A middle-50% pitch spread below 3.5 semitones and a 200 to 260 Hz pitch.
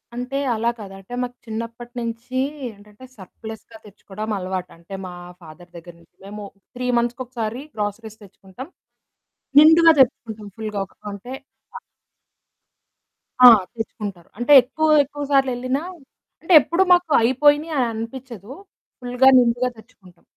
No: average, 3.8 semitones; high, 230 Hz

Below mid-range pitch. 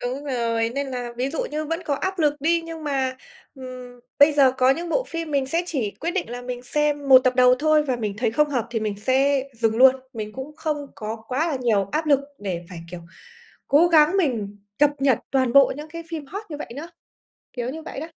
No: very high, 270 Hz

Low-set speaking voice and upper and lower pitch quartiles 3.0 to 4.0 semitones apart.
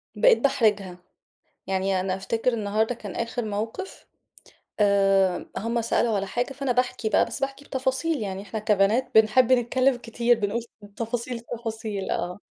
No: high, 225 Hz; average, 3.5 semitones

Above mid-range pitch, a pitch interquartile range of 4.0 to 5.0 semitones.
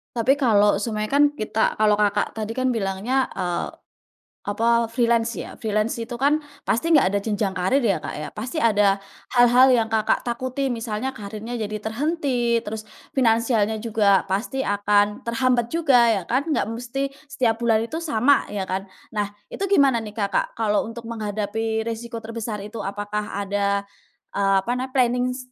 No: high, 225 Hz; average, 3.0 semitones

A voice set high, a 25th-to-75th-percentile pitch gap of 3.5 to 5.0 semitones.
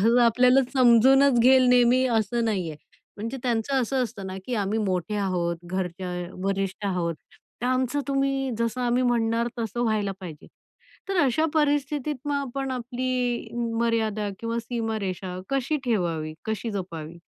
Yes: high, 230 Hz; average, 4.6 semitones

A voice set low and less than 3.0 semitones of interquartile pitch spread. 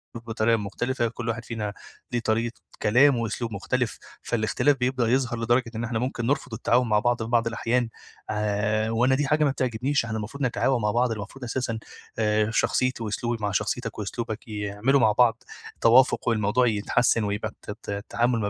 Yes: low, 115 Hz; narrow, 2.4 semitones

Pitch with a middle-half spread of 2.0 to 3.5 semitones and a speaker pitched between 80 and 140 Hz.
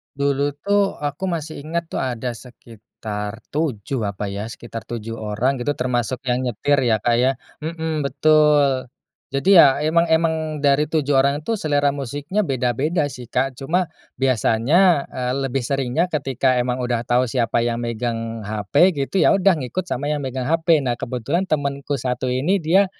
No: average, 4.1 semitones; low, 135 Hz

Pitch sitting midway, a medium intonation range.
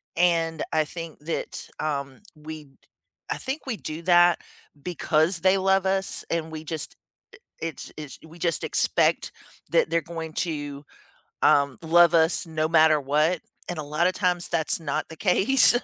No: medium, 165 Hz; narrow, 2.2 semitones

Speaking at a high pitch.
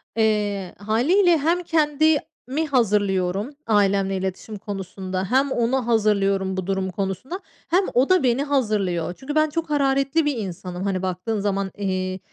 Yes: high, 210 Hz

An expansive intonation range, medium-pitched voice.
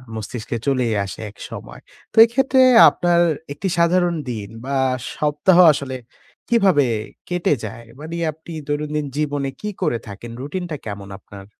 Yes: wide, 6.8 semitones; medium, 150 Hz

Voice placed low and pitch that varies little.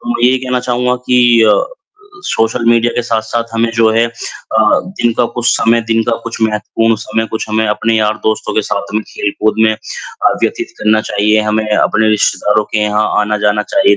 Yes: low, 110 Hz; narrow, 1.5 semitones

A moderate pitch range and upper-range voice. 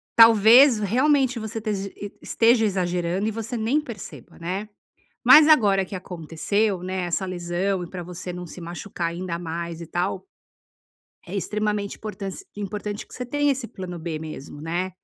Yes: average, 3.9 semitones; high, 195 Hz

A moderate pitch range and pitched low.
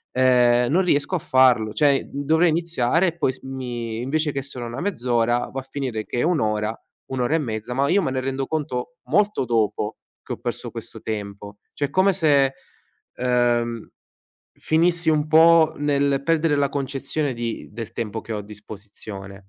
Yes: average, 4.8 semitones; low, 130 Hz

